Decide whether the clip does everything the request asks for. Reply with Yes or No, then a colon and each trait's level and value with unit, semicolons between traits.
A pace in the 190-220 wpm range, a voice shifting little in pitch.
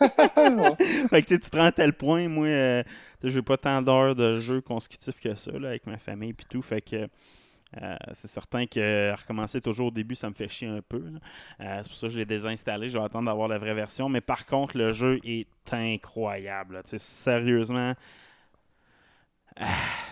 No: fast, 205 wpm; average, 3.3 semitones